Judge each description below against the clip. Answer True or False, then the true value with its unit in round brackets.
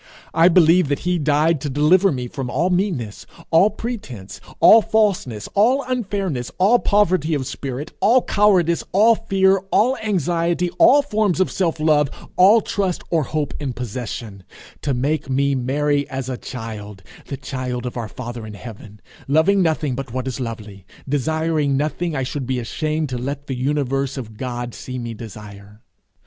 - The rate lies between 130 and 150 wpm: False (165 wpm)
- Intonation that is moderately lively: False (6.4 semitones)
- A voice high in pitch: False (145 Hz)